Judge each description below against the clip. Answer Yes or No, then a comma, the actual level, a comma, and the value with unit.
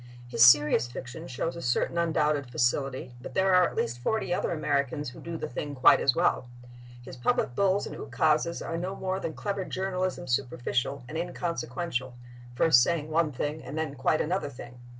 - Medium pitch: Yes, medium, 150 Hz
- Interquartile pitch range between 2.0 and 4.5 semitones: No, average, 5.2 semitones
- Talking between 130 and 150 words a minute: No, average, 180 wpm